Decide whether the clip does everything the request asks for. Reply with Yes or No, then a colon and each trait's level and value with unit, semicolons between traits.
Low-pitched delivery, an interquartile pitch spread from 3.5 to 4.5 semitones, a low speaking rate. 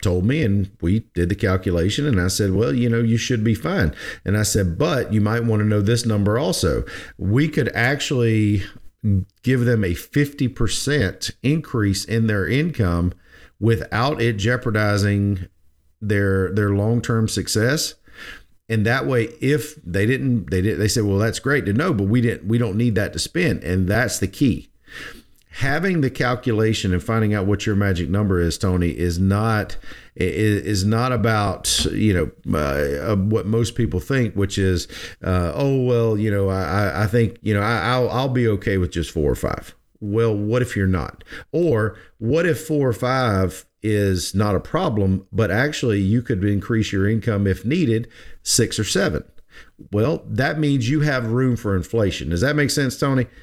No: low, 110 Hz; average, 3.9 semitones; average, 180 wpm